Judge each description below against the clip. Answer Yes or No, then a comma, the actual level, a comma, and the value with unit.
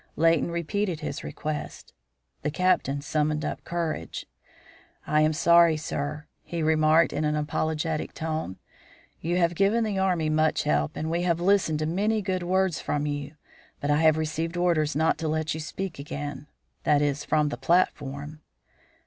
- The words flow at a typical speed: Yes, average, 165 wpm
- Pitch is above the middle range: No, medium, 155 Hz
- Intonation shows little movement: Yes, narrow, 2.3 semitones